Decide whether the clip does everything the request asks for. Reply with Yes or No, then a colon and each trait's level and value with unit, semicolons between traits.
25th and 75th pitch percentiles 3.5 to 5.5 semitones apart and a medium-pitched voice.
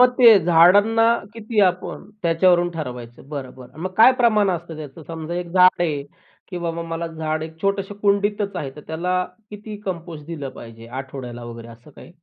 Yes: average, 4.7 semitones; medium, 170 Hz